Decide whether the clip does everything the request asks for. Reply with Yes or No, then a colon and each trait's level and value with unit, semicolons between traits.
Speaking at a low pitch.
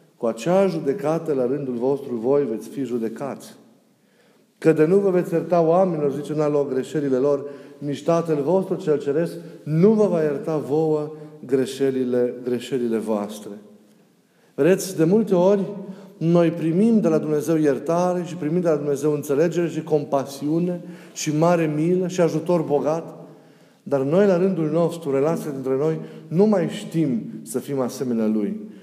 No: medium, 155 Hz